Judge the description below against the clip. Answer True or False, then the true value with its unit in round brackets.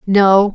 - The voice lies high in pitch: True (195 Hz)